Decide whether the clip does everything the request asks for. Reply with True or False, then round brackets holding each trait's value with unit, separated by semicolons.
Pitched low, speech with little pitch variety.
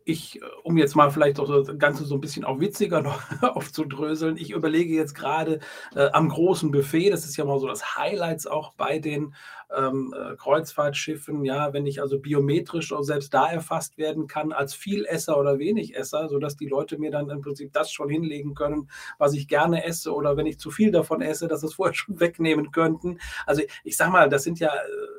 False (150 Hz; 2.0 semitones)